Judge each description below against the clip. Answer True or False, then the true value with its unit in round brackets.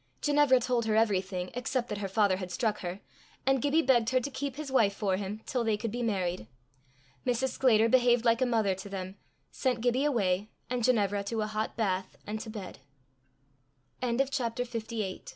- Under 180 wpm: False (200 wpm)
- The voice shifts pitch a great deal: False (3.8 semitones)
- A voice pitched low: False (225 Hz)